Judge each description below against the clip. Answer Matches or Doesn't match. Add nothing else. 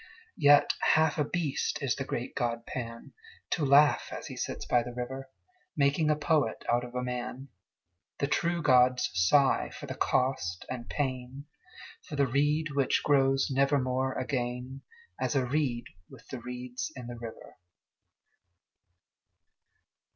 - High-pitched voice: Doesn't match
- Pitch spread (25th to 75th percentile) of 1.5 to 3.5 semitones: Matches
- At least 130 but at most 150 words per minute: Matches